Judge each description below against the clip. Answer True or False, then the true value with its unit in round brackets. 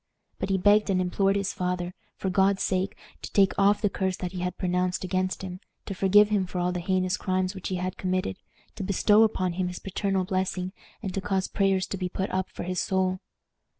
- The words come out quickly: True (220 wpm)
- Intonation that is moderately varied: False (1.2 semitones)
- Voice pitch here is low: False (185 Hz)